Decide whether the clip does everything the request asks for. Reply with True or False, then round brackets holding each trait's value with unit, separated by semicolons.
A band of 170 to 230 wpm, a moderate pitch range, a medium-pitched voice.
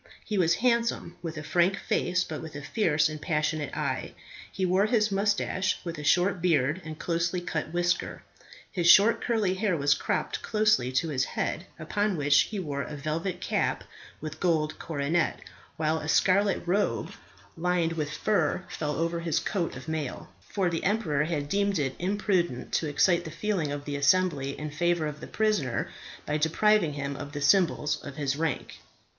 True (180 wpm; 3.9 semitones; 165 Hz)